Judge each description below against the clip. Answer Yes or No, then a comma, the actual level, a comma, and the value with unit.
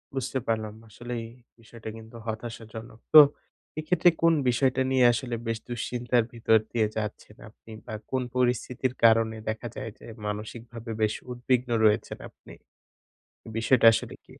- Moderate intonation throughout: No, narrow, 1.9 semitones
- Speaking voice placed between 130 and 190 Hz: No, low, 115 Hz